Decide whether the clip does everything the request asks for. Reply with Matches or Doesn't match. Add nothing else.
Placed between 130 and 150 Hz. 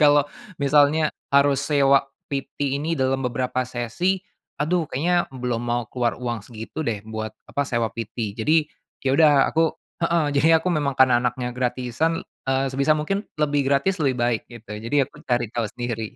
Matches